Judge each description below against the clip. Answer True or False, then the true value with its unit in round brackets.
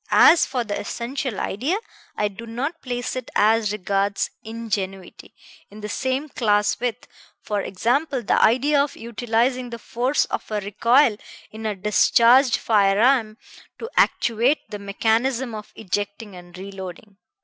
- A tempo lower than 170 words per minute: True (140 wpm)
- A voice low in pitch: False (225 Hz)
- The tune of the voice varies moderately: True (3.5 semitones)